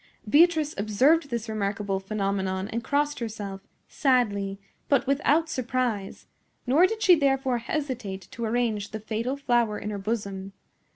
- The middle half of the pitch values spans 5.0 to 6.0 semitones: Yes, wide, 5.5 semitones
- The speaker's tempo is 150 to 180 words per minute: No, slow, 135 wpm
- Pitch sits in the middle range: No, high, 230 Hz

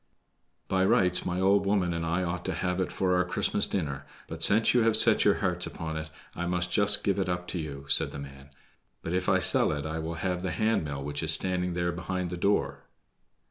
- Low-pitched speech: Yes, very low, 90 Hz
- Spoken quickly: Yes, fast, 235 wpm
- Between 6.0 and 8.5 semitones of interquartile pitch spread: No, narrow, 2.6 semitones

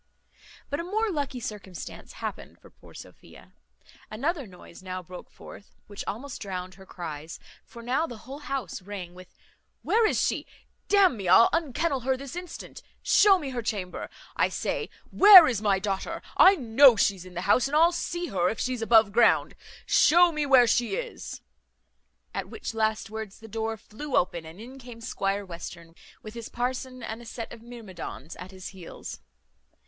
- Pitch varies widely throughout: Yes, wide, 6.2 semitones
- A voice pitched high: Yes, high, 225 Hz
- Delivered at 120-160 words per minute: No, average, 180 wpm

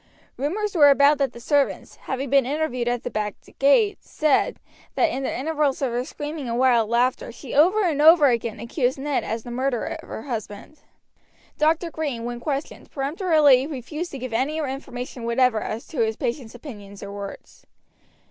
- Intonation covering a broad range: No, average, 4.0 semitones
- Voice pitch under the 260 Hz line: No, very high, 265 Hz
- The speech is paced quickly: No, average, 180 wpm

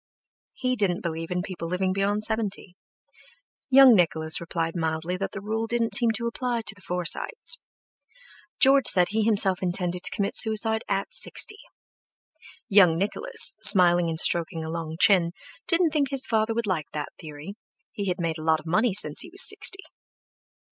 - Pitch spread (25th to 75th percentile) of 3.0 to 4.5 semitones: No, average, 5.0 semitones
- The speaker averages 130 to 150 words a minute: No, average, 170 wpm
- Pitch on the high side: Yes, high, 195 Hz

